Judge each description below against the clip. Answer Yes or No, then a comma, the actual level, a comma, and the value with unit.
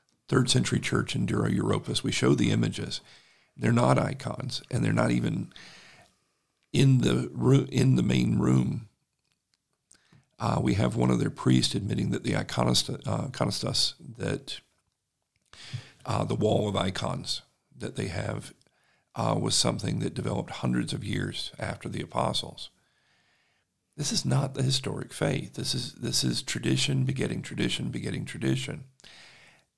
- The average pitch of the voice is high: No, very low, 95 Hz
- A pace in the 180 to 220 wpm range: No, average, 145 wpm